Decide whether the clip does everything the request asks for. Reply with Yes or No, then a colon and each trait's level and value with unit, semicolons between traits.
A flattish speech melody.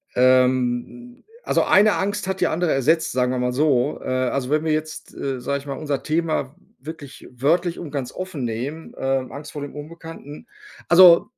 No: average, 4.2 semitones